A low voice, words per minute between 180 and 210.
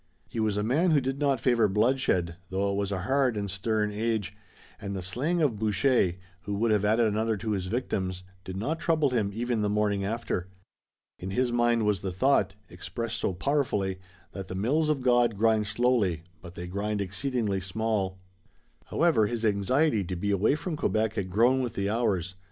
Yes: low, 110 Hz; average, 190 wpm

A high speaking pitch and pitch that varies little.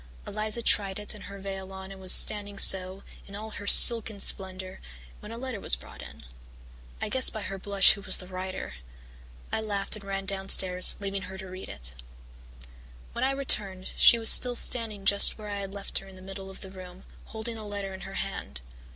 Yes: high, 195 Hz; narrow, 1.9 semitones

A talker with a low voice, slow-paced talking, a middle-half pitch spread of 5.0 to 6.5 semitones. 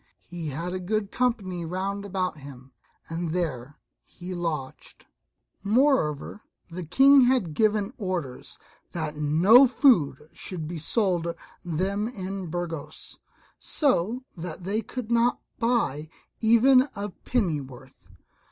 No: medium, 185 Hz; slow, 115 wpm; wide, 5.6 semitones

